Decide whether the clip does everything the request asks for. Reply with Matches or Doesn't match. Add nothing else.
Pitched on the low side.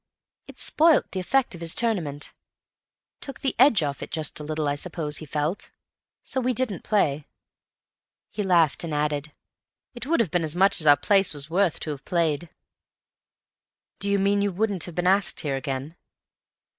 Doesn't match